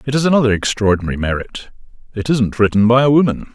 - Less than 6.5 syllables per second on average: No, 6.8 syllables/s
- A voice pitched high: No, low, 115 Hz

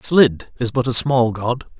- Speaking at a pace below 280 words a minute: Yes, average, 200 wpm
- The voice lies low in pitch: Yes, low, 125 Hz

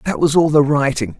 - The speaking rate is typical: No, fast, 250 wpm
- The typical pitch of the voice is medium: Yes, medium, 150 Hz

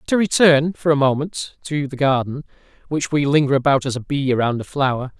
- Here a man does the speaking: Yes, male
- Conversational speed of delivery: No, fast, 210 wpm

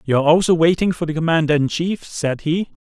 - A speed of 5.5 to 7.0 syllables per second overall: Yes, 5.7 syllables/s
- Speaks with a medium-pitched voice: Yes, medium, 160 Hz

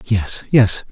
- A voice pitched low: Yes, low, 110 Hz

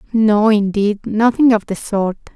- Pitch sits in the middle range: No, high, 215 Hz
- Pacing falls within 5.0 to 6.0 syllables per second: No, 4.3 syllables/s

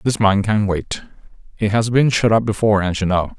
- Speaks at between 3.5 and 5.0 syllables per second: No, 5.5 syllables/s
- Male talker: Yes, male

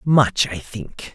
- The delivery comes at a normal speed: Yes, average, 155 wpm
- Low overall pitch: Yes, low, 115 Hz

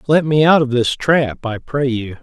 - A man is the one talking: Yes, male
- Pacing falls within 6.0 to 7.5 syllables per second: No, 4.4 syllables/s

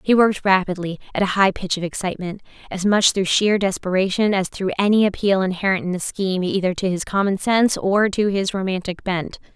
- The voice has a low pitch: No, high, 190 Hz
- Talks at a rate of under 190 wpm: No, average, 195 wpm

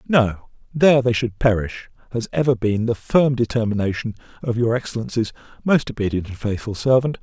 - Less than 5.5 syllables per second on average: No, 5.6 syllables/s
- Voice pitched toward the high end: No, low, 120 Hz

